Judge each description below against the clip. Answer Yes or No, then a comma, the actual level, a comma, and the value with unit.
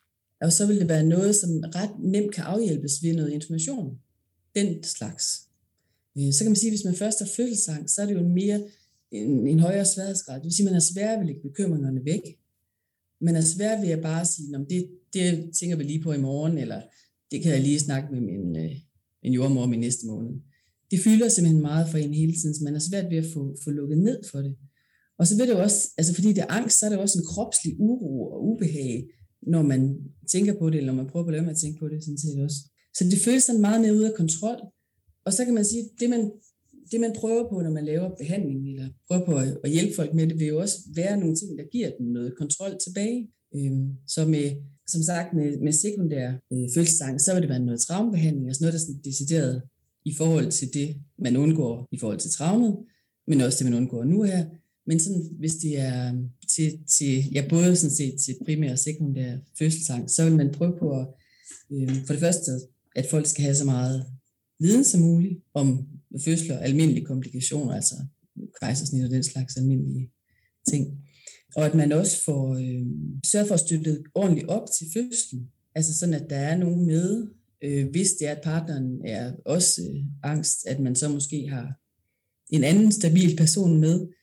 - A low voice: No, medium, 155 Hz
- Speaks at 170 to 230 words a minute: Yes, average, 215 wpm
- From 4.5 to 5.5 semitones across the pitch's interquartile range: Yes, average, 4.8 semitones